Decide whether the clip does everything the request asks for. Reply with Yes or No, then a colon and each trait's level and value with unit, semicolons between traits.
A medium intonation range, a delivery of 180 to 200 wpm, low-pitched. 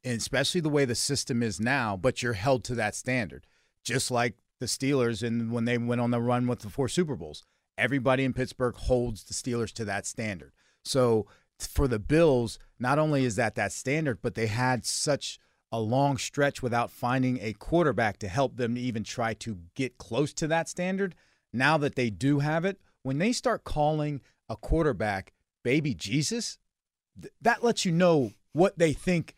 Yes: average, 3.8 semitones; average, 190 wpm; low, 125 Hz